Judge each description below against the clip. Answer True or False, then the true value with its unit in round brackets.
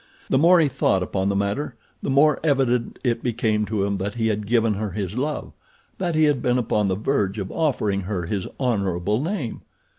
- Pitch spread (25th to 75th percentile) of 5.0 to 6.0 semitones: True (5.4 semitones)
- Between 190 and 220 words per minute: True (200 wpm)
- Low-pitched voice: True (110 Hz)